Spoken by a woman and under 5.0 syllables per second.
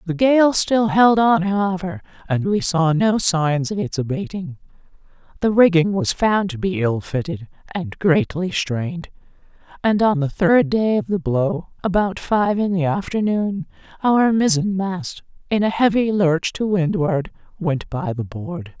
Yes: female; 4.2 syllables/s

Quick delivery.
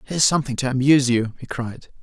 Yes: fast, 210 wpm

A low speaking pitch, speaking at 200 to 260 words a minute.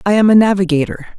No: high, 190 Hz; fast, 205 wpm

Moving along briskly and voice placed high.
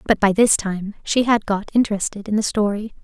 Yes: fast, 220 wpm; high, 210 Hz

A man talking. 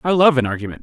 Yes: male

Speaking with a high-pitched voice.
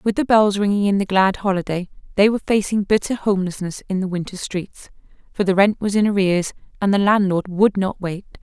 Yes: high, 195 Hz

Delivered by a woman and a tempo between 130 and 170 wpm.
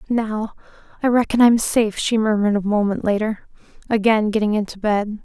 Yes: female; average, 160 wpm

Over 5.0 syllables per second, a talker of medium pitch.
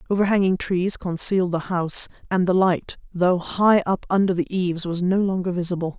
Yes: 5.4 syllables/s; medium, 180 Hz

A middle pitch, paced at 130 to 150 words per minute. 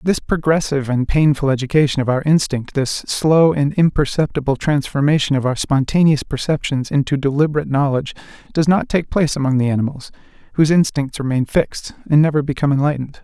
No: medium, 145 Hz; average, 160 wpm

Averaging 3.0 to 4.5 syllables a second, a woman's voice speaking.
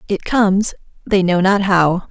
Yes: 4.4 syllables/s; female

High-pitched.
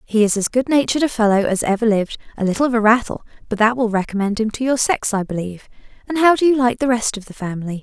Yes: high, 225 Hz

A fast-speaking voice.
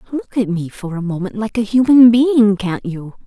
Yes: fast, 220 wpm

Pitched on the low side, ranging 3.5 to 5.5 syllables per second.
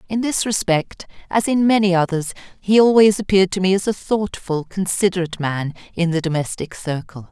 No: medium, 185 Hz; 5.4 syllables/s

